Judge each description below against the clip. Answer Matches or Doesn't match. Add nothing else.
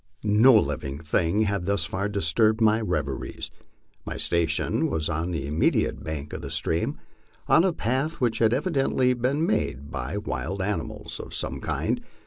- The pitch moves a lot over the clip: Matches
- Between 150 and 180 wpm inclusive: Matches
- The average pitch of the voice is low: Matches